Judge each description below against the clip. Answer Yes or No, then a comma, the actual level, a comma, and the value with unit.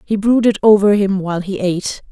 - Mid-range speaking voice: No, high, 200 Hz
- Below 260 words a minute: Yes, average, 200 wpm